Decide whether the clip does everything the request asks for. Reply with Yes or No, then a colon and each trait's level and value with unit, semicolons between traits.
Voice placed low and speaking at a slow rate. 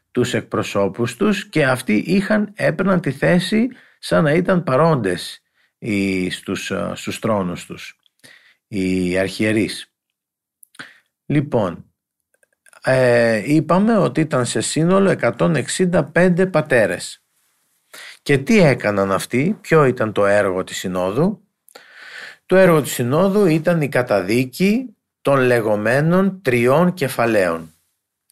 Yes: low, 130 Hz; slow, 105 wpm